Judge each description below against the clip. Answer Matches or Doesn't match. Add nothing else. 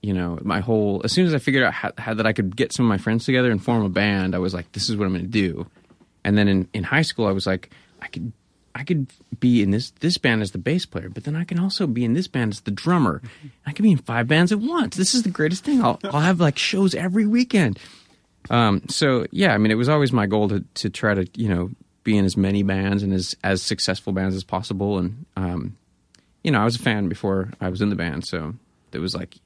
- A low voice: Matches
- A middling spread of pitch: Doesn't match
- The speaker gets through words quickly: Matches